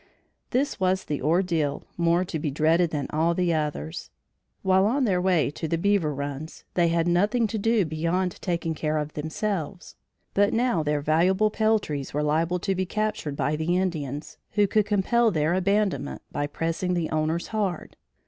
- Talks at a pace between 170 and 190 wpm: Yes, average, 175 wpm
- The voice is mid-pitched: Yes, medium, 170 Hz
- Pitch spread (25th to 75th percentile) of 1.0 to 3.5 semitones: No, average, 4.0 semitones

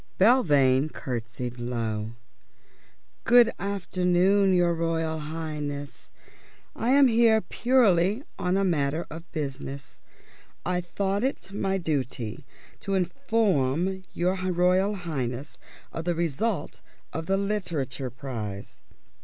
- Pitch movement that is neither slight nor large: No, wide, 5.8 semitones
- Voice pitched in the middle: Yes, medium, 170 Hz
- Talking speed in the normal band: No, slow, 105 wpm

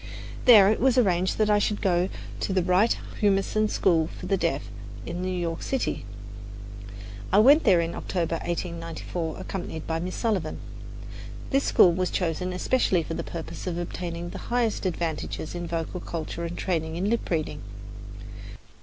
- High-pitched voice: No, medium, 180 Hz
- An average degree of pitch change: Yes, average, 3.2 semitones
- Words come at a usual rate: Yes, average, 165 wpm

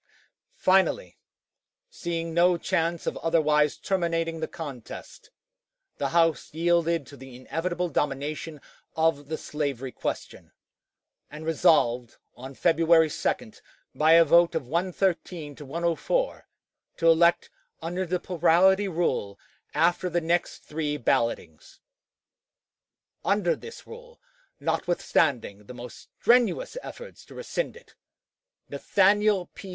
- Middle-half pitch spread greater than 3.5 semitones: No, average, 3.1 semitones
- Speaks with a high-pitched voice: No, medium, 165 Hz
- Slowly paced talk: Yes, slow, 115 wpm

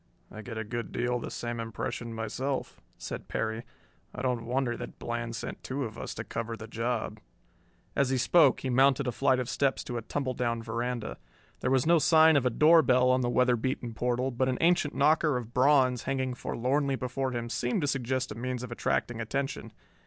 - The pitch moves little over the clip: Yes, narrow, 2.2 semitones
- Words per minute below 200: No, fast, 205 wpm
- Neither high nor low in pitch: No, low, 125 Hz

